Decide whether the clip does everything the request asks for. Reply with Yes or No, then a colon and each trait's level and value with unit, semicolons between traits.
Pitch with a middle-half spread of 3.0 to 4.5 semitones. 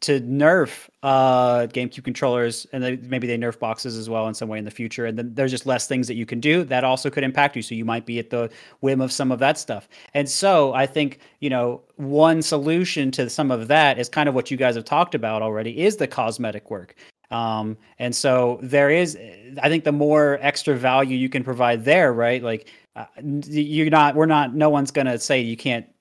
Yes: average, 3.4 semitones